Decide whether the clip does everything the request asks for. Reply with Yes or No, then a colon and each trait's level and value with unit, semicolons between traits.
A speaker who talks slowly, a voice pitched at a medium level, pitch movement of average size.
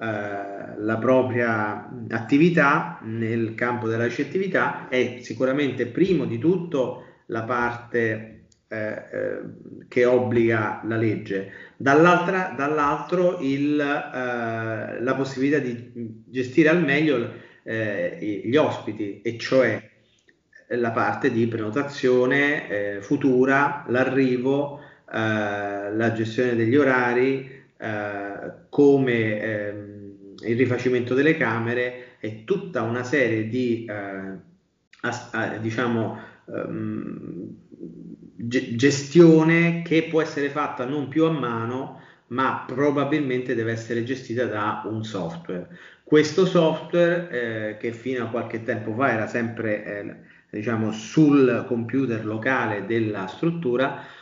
No: slow, 110 wpm; low, 125 Hz; average, 4.1 semitones